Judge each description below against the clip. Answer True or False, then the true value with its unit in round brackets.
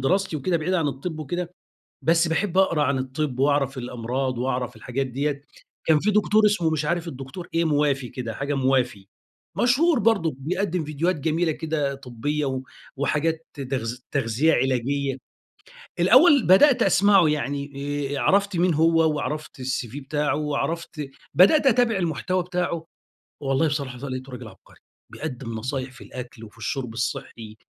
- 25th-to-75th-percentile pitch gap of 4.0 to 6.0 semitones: True (4.4 semitones)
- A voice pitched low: False (145 Hz)